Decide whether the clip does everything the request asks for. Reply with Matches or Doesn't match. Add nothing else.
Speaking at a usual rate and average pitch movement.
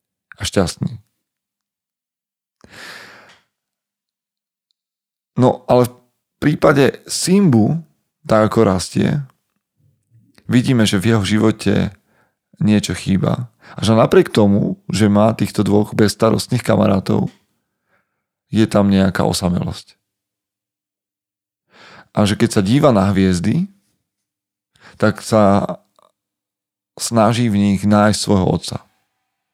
Doesn't match